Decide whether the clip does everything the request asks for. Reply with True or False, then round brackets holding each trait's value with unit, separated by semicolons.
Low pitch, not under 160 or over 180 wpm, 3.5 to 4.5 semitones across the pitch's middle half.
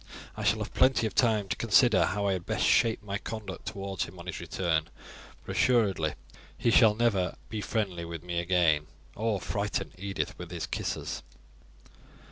True (100 Hz; 175 wpm; 3.9 semitones)